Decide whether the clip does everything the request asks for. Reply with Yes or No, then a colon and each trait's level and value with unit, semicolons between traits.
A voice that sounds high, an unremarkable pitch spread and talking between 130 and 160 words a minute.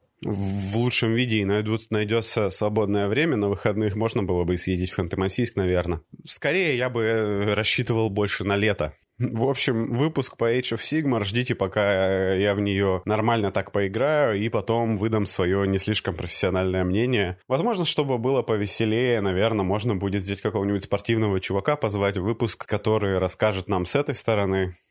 No: low, 105 Hz; average, 3.0 semitones; average, 155 wpm